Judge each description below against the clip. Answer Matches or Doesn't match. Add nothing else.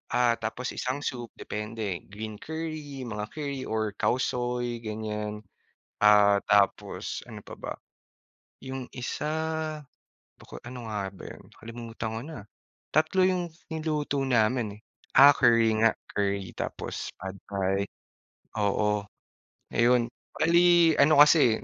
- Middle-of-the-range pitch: Doesn't match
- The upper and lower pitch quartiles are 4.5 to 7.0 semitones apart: Matches